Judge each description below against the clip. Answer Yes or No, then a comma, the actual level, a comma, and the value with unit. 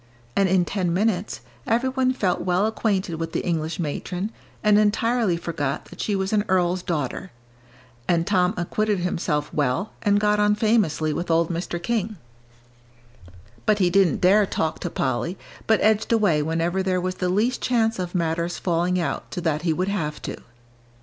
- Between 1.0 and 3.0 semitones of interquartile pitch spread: No, average, 3.7 semitones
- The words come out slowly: No, average, 175 wpm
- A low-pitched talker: No, medium, 185 Hz